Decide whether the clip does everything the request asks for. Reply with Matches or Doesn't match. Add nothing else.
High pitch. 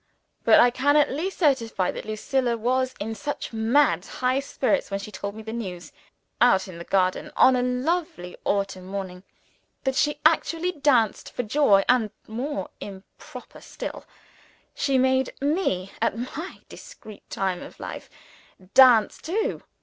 Matches